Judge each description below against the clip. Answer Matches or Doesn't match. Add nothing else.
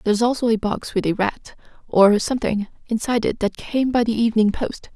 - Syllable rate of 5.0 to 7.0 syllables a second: Matches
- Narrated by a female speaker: Matches